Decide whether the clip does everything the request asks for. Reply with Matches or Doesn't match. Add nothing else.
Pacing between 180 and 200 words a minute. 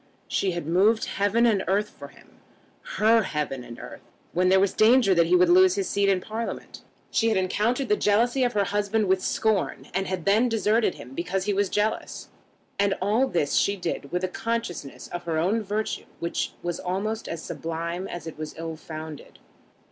Matches